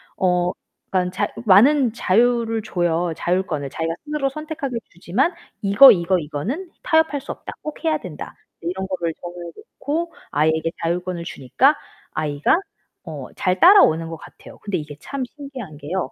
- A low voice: No, medium, 185 Hz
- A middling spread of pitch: No, wide, 8.4 semitones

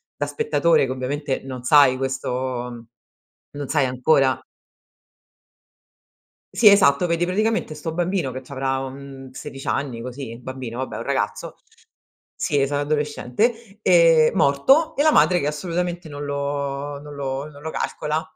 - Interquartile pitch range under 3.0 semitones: No, average, 3.7 semitones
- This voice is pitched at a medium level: Yes, medium, 145 Hz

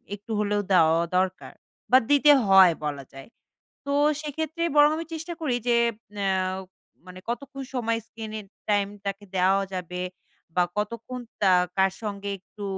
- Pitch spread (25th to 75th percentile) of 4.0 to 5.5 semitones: Yes, average, 5.1 semitones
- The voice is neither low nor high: No, high, 205 Hz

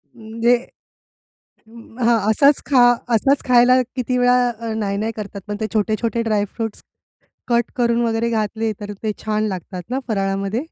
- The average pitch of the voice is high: Yes, high, 225 Hz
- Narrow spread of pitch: Yes, narrow, 2.2 semitones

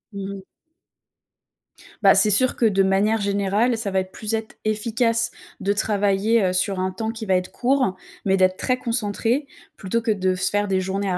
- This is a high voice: Yes, high, 205 Hz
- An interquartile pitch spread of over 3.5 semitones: No, average, 2.9 semitones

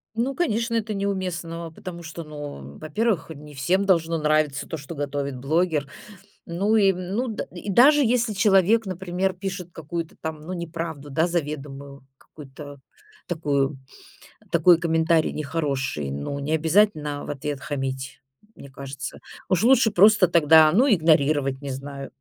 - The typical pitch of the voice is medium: Yes, medium, 160 Hz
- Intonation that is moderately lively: Yes, average, 4.8 semitones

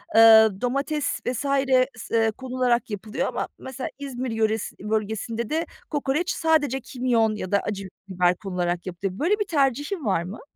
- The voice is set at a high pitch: Yes, high, 235 Hz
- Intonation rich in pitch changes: No, average, 4.6 semitones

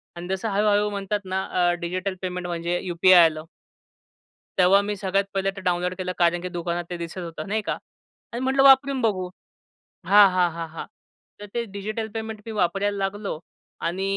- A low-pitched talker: No, high, 190 Hz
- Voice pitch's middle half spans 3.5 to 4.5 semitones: No, average, 2.8 semitones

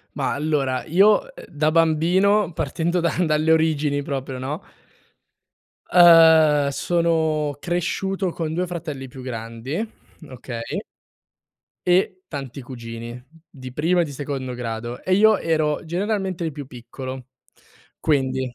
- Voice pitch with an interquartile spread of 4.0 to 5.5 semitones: Yes, average, 4.6 semitones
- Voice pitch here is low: No, medium, 150 Hz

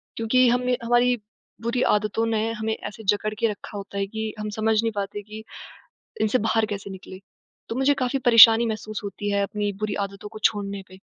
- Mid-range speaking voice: No, high, 215 Hz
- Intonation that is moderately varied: No, narrow, 2.0 semitones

